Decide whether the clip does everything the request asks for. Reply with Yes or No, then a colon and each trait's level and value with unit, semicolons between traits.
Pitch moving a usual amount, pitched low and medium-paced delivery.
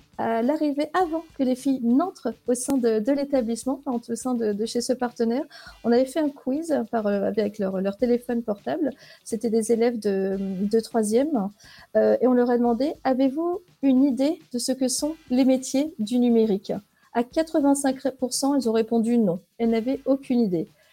No: average, 3.2 semitones; high, 245 Hz; average, 180 wpm